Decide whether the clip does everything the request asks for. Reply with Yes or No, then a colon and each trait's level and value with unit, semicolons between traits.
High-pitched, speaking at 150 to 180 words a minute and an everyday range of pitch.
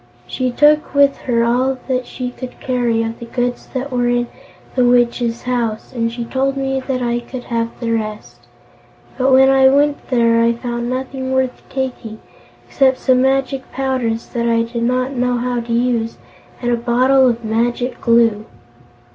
No: high, 245 Hz; average, 170 wpm; narrow, 2.0 semitones